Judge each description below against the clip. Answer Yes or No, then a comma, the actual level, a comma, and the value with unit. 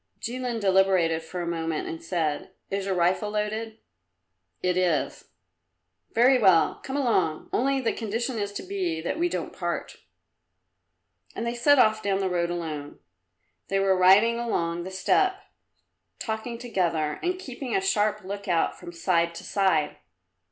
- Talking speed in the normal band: Yes, average, 155 wpm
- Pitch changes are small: No, average, 5.3 semitones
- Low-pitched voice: No, high, 195 Hz